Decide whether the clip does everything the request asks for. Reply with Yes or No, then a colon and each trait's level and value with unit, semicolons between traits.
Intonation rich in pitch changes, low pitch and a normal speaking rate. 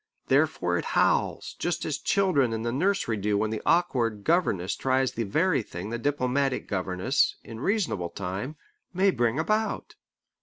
Yes: wide, 7.1 semitones; low, 125 Hz; average, 155 wpm